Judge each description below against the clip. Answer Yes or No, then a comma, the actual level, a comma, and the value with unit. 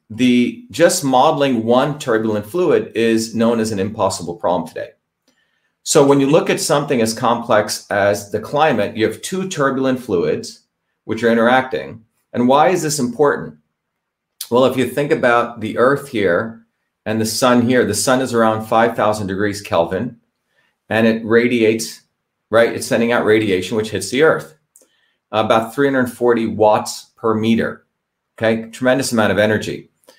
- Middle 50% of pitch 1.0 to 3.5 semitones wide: Yes, average, 2.8 semitones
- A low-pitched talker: Yes, low, 115 Hz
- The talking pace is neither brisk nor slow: Yes, average, 155 wpm